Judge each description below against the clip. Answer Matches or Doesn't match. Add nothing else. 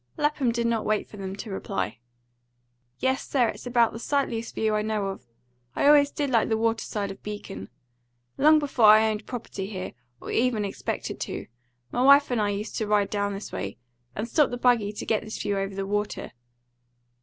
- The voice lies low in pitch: Doesn't match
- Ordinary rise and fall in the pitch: Matches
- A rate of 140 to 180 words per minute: Doesn't match